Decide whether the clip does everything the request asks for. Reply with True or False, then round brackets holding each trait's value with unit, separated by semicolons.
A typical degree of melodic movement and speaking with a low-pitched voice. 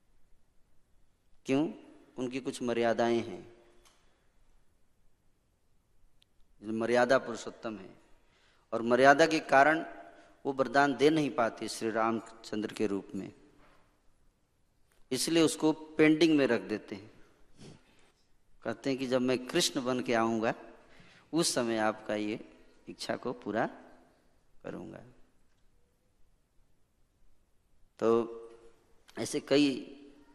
True (4.2 semitones; 115 Hz)